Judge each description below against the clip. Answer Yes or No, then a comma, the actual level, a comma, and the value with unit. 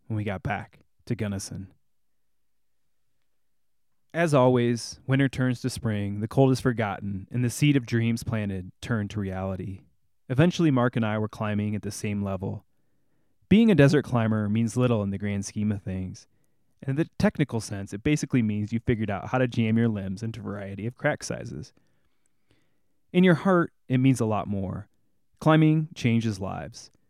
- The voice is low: Yes, low, 115 Hz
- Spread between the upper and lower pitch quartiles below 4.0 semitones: No, average, 4.4 semitones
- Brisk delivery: No, average, 175 wpm